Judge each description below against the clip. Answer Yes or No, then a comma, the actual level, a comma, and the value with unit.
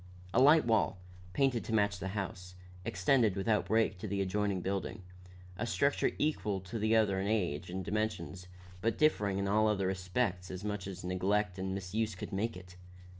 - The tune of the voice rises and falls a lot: No, average, 2.9 semitones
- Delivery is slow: No, average, 180 wpm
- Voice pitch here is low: Yes, low, 100 Hz